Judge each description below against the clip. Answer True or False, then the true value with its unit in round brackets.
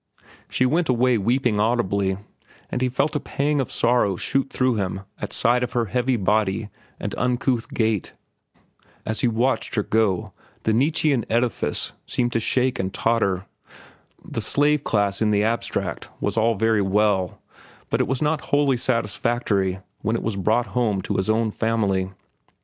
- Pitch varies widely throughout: False (3.5 semitones)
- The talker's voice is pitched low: True (115 Hz)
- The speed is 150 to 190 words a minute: True (165 wpm)